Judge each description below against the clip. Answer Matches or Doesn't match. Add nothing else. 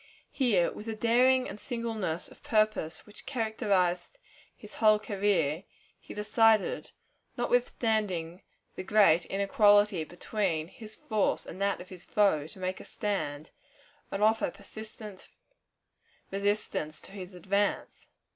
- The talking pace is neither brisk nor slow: Doesn't match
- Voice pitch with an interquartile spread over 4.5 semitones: Doesn't match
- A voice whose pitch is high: Matches